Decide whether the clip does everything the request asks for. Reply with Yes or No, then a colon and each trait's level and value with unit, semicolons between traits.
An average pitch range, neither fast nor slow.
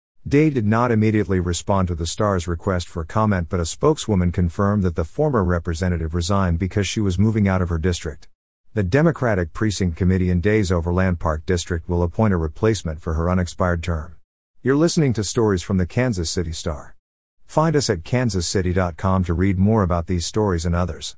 Yes: average, 3.6 semitones; average, 185 wpm